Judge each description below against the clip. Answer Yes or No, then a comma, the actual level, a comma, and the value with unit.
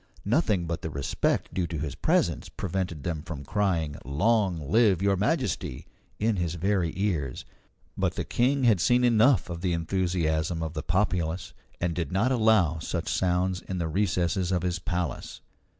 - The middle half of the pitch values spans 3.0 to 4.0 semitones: Yes, average, 3.5 semitones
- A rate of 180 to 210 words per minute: No, average, 165 wpm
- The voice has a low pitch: Yes, very low, 90 Hz